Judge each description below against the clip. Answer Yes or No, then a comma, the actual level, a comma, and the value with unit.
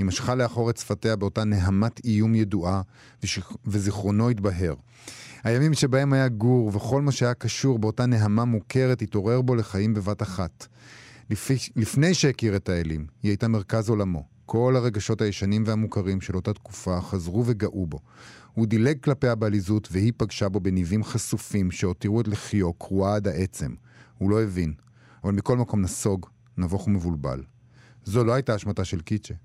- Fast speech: Yes, fast, 155 wpm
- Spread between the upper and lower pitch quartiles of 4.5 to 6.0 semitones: No, average, 3.3 semitones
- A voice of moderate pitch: No, low, 110 Hz